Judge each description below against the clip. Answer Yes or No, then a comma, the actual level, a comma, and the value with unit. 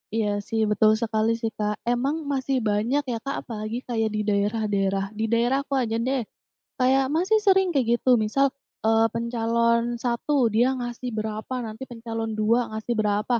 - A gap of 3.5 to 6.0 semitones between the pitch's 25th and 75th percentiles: No, average, 2.7 semitones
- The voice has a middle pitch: No, high, 230 Hz